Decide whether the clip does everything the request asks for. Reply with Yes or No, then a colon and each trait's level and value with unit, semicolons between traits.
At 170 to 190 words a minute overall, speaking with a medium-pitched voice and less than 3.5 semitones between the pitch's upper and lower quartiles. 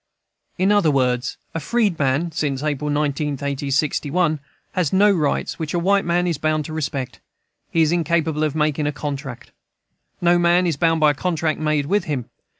Yes: average, 175 wpm; medium, 155 Hz; average, 3.0 semitones